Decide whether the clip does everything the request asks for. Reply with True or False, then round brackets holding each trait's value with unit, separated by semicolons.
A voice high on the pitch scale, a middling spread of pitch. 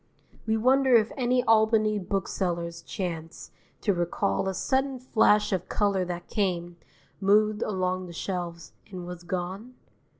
True (195 Hz; 3.7 semitones)